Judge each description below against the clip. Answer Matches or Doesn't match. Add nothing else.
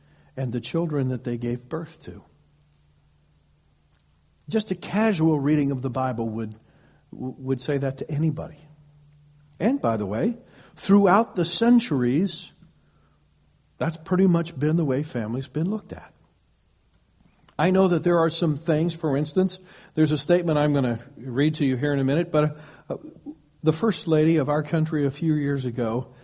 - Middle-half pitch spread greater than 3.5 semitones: Matches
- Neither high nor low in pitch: Matches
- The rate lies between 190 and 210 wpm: Doesn't match